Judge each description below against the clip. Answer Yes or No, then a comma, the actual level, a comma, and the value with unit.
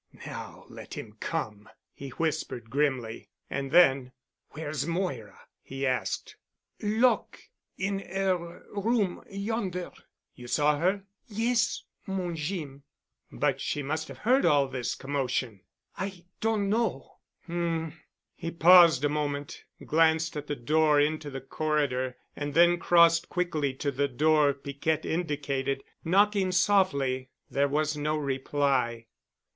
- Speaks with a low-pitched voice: No, medium, 155 Hz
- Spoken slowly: Yes, slow, 125 wpm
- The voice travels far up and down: No, average, 4.5 semitones